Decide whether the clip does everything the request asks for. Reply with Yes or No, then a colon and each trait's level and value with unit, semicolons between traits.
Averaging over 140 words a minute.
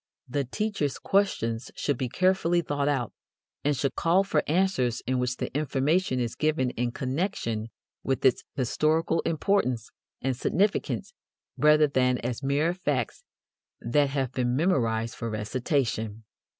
No: slow, 135 wpm